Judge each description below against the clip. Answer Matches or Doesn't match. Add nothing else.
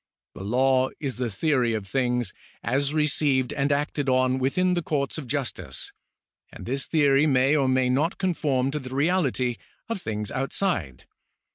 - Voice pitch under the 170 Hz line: Matches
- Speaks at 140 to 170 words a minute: Matches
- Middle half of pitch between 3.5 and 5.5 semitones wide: Doesn't match